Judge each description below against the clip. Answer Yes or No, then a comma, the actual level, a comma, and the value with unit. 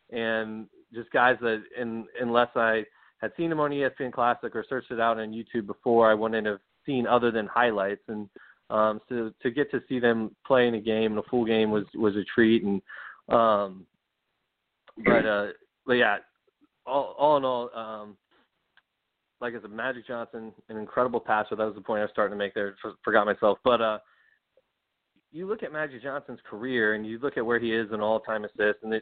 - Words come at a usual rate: No, fast, 210 wpm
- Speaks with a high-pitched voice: No, low, 115 Hz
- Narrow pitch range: Yes, narrow, 2.2 semitones